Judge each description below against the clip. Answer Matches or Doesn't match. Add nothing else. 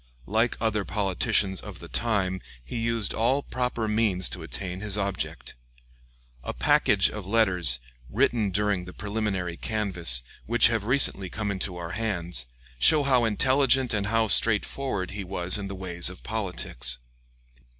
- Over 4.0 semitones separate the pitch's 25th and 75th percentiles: Doesn't match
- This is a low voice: Matches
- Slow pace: Doesn't match